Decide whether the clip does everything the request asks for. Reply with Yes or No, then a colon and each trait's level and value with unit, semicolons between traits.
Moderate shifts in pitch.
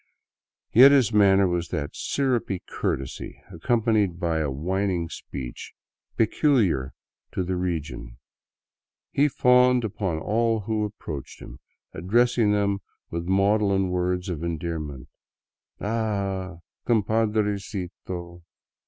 Yes: average, 4.3 semitones